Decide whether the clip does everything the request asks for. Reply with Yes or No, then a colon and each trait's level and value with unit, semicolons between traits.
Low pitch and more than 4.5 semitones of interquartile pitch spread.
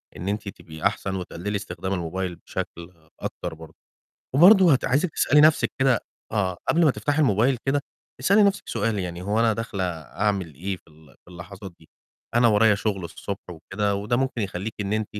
Yes: low, 100 Hz; average, 5.1 semitones